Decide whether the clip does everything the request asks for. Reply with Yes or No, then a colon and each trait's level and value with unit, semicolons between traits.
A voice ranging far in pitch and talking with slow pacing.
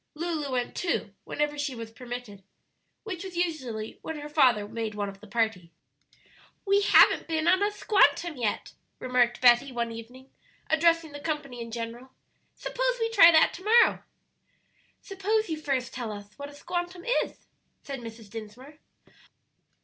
No: wide, 6.4 semitones; average, 155 wpm